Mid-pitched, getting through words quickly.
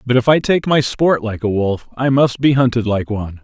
No: low, 120 Hz; fast, 260 wpm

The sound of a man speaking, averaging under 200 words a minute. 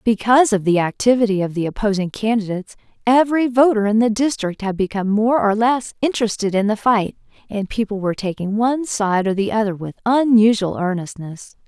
No: female; average, 175 wpm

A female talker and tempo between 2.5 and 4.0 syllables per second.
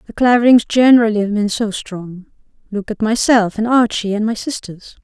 No: female; 5.3 syllables/s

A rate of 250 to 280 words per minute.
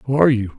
No: fast, 305 wpm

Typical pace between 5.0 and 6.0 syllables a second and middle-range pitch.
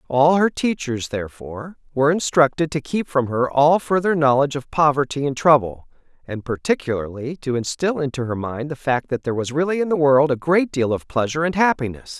Yes: 5.7 syllables/s; medium, 145 Hz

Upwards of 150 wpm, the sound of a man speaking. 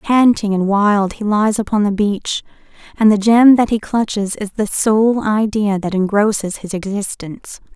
No: average, 170 wpm; female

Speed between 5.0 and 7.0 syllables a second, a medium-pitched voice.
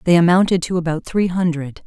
Yes: 5.7 syllables/s; medium, 170 Hz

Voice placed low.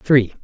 Yes: low, 125 Hz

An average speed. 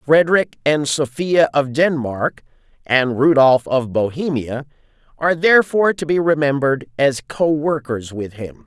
No: slow, 125 wpm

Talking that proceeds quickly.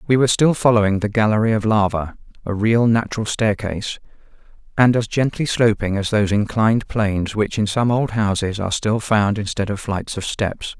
No: average, 185 wpm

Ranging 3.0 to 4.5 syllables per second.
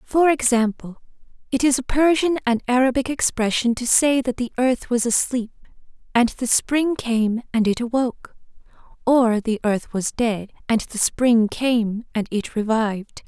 Yes: 4.4 syllables/s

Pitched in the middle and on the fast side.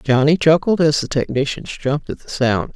No: medium, 145 Hz; average, 195 wpm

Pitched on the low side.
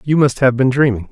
Yes: low, 130 Hz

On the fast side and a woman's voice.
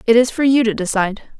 Yes: fast, 260 wpm; female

